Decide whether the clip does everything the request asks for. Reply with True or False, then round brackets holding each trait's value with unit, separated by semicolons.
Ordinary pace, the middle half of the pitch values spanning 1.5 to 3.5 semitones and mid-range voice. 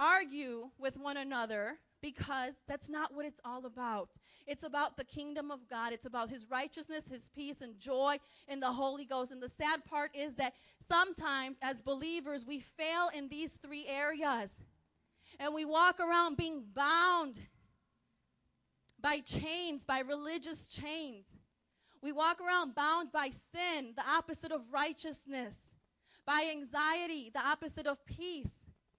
False (145 wpm; 2.7 semitones; 290 Hz)